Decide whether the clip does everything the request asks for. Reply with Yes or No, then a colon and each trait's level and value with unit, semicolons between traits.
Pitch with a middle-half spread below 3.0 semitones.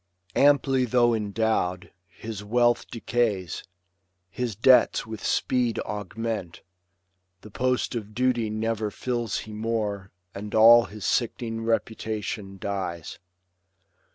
Yes: narrow, 2.5 semitones